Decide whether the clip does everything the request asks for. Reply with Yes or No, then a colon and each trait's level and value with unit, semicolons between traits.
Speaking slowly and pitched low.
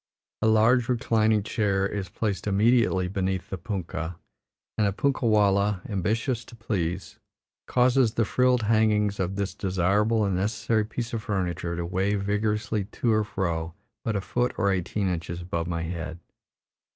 No: average, 155 wpm; low, 105 Hz